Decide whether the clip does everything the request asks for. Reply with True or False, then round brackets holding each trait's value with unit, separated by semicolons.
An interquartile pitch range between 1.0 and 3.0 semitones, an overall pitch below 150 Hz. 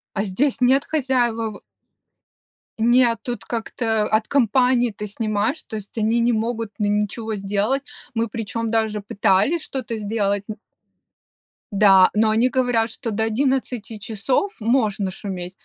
False (2.7 semitones; 225 Hz)